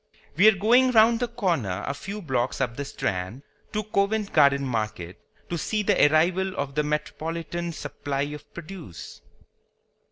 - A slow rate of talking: No, average, 155 wpm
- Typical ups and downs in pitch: No, wide, 6.4 semitones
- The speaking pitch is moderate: Yes, medium, 155 Hz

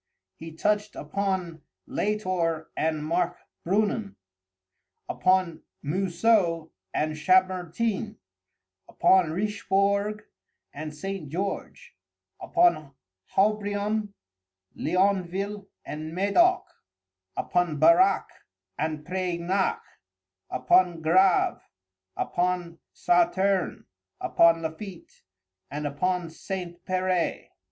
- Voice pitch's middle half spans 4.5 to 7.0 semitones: No, average, 3.3 semitones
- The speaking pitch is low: No, medium, 185 Hz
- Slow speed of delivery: Yes, slow, 75 wpm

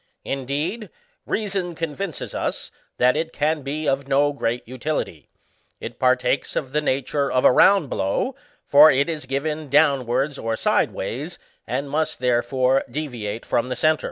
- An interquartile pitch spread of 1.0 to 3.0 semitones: No, average, 3.5 semitones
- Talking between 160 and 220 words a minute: No, average, 150 wpm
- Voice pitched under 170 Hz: Yes, medium, 140 Hz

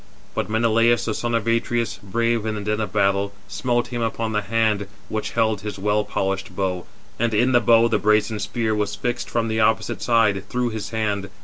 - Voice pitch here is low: Yes, low, 110 Hz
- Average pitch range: No, narrow, 2.0 semitones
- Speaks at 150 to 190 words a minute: No, fast, 205 wpm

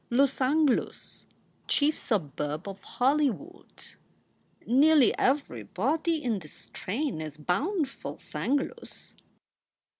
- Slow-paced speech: Yes, slow, 90 wpm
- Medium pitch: No, very high, 265 Hz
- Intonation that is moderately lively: No, wide, 7.5 semitones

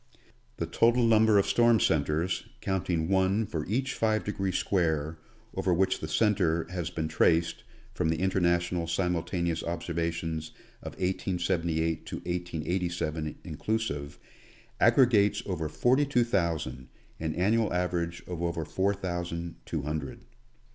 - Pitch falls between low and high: No, very low, 85 Hz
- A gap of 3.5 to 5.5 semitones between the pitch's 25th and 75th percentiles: No, average, 3.0 semitones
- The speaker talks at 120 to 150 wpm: Yes, slow, 135 wpm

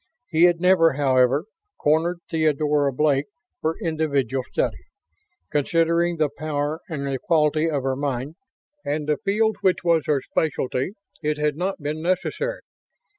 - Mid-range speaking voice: Yes, medium, 155 Hz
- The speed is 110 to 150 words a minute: Yes, average, 140 wpm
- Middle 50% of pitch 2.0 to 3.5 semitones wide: Yes, average, 2.8 semitones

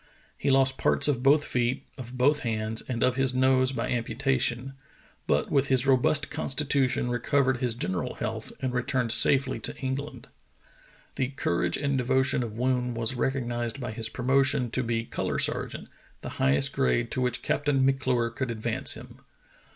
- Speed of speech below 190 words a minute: Yes, average, 165 wpm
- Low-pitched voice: Yes, low, 130 Hz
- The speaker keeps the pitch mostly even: Yes, narrow, 2.3 semitones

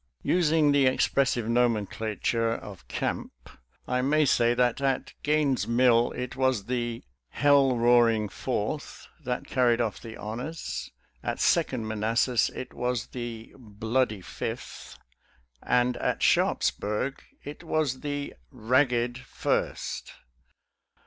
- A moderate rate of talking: No, slow, 125 wpm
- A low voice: Yes, low, 125 Hz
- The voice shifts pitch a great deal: No, average, 2.7 semitones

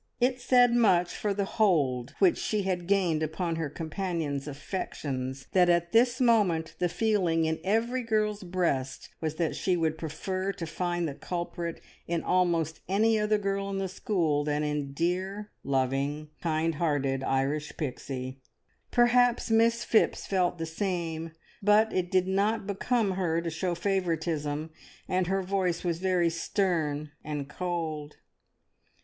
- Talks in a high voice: No, medium, 175 Hz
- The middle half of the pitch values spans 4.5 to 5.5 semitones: No, average, 4.1 semitones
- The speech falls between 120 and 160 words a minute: Yes, average, 150 wpm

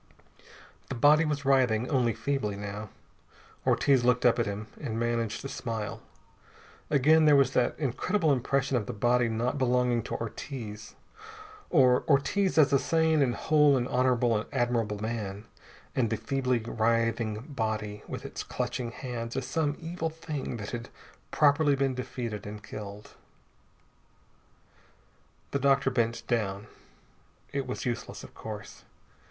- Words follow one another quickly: No, average, 140 wpm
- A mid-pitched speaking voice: No, low, 125 Hz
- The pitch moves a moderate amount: Yes, average, 3.6 semitones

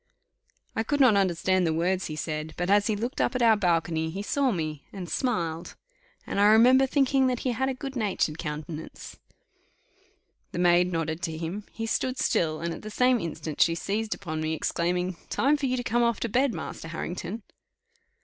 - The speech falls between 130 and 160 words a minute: No, average, 195 wpm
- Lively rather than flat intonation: Yes, wide, 6.5 semitones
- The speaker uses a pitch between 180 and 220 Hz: Yes, high, 190 Hz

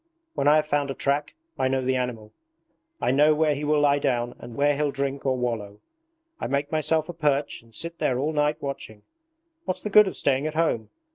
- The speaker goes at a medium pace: No, fast, 220 wpm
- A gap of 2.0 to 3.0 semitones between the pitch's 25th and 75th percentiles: Yes, average, 2.7 semitones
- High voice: No, medium, 140 Hz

